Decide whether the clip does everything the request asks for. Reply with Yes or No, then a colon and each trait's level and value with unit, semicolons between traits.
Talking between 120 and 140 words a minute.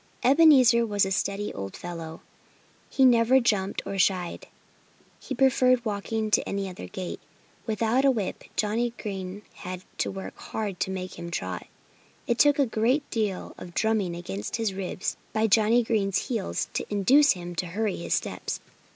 No: average, 160 wpm